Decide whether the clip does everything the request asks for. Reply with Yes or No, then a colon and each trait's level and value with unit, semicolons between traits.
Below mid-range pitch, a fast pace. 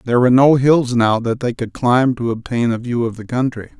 Yes: low, 120 Hz; fast, 255 wpm